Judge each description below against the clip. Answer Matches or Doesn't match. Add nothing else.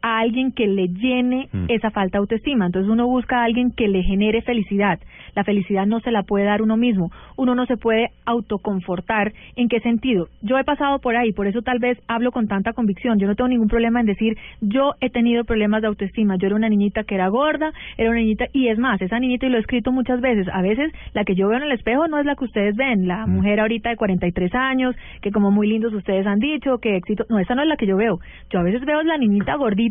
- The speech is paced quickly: Matches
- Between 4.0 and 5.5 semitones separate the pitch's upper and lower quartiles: Doesn't match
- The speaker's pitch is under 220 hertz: Doesn't match